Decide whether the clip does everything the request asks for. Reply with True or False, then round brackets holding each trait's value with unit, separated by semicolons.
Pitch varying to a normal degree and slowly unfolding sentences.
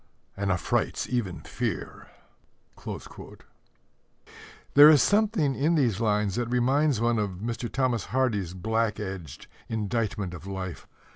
True (4.8 semitones; 120 wpm)